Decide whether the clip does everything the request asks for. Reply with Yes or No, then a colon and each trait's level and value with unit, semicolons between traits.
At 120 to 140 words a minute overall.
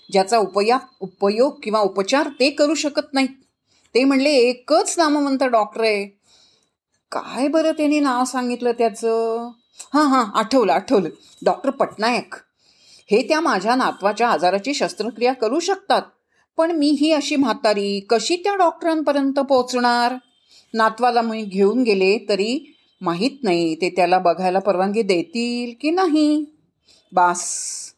Yes: fast, 130 wpm